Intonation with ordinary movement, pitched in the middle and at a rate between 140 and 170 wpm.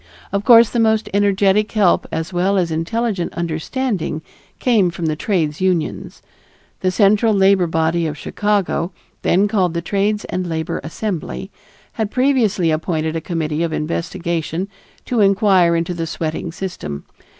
Yes: average, 3.9 semitones; medium, 180 Hz; average, 145 wpm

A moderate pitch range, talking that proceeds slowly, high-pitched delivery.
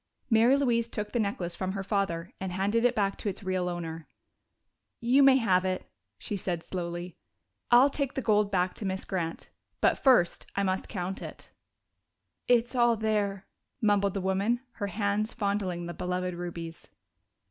No: average, 3.8 semitones; average, 170 wpm; high, 195 Hz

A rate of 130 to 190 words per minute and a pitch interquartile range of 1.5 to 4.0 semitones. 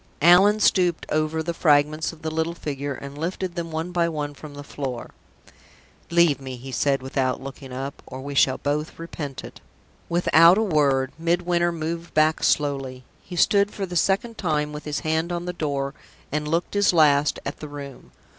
Yes: average, 185 wpm; average, 3.3 semitones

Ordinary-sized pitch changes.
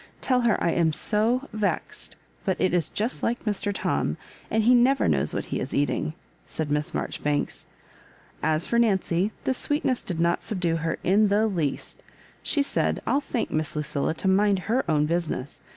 No: wide, 6.2 semitones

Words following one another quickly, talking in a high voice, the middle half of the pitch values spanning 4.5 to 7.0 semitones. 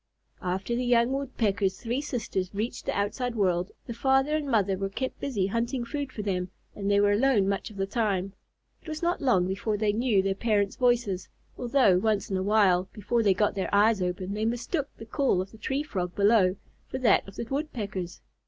No: fast, 210 wpm; high, 210 Hz; average, 4.1 semitones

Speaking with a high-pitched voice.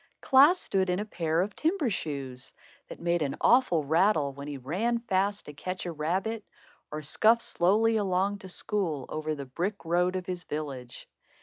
No: medium, 180 Hz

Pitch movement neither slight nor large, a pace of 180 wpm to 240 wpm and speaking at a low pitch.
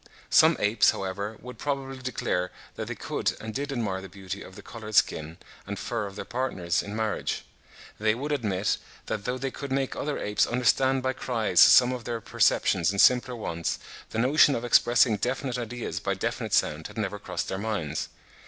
Yes: average, 4.3 semitones; average, 190 wpm; low, 110 Hz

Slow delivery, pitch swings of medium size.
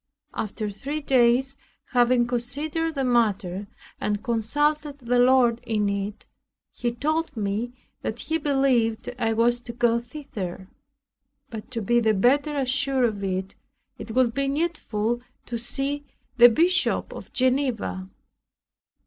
Yes: slow, 130 wpm; average, 3.7 semitones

